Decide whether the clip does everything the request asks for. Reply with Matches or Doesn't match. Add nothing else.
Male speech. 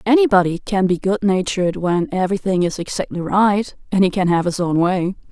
Doesn't match